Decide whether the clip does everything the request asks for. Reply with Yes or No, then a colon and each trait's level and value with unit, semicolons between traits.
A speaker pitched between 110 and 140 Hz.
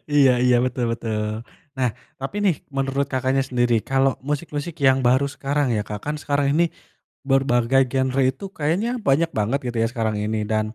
Yes: low, 135 Hz